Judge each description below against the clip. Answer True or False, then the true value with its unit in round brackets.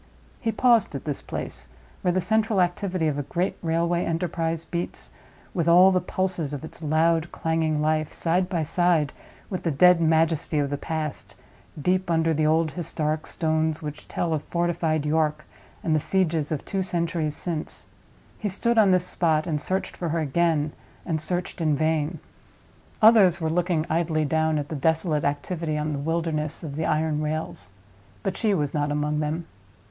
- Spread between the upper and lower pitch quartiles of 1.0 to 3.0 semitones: True (2.4 semitones)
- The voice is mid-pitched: True (160 Hz)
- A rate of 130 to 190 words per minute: True (175 wpm)